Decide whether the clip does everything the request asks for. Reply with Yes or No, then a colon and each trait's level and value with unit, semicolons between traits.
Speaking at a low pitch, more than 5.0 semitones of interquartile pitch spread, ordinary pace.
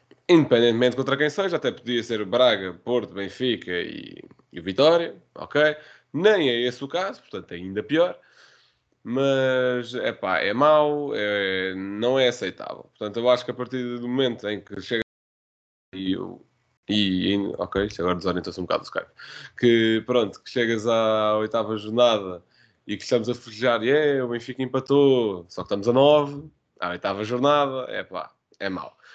No: low, 120 Hz; average, 4.3 semitones; average, 165 wpm